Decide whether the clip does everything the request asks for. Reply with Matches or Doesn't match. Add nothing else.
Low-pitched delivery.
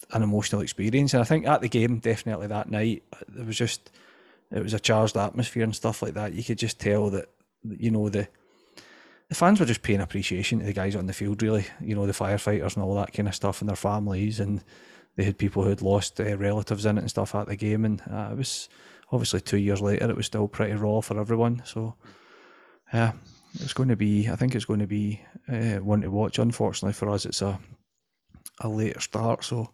Matches